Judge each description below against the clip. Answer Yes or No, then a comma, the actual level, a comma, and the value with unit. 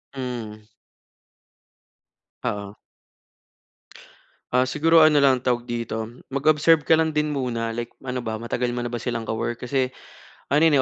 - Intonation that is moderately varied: Yes, average, 3.7 semitones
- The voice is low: Yes, low, 125 Hz